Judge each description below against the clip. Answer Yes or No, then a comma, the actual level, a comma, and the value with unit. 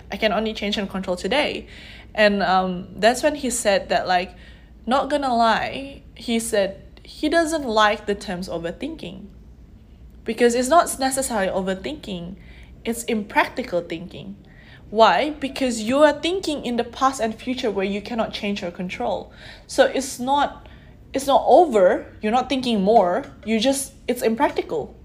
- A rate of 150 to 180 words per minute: Yes, average, 155 wpm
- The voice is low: No, high, 225 Hz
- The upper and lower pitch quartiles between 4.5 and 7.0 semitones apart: Yes, average, 5.1 semitones